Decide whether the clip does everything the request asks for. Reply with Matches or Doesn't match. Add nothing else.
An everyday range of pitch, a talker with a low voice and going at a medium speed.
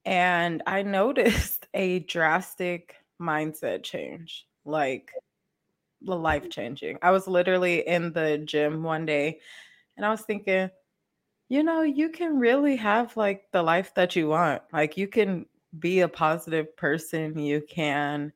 Doesn't match